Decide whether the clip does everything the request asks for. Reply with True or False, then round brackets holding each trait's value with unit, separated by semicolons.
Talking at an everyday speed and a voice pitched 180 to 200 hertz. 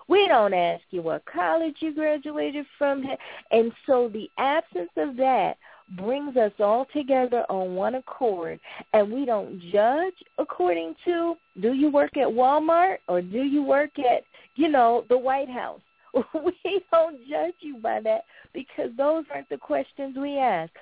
False (160 wpm; 265 Hz)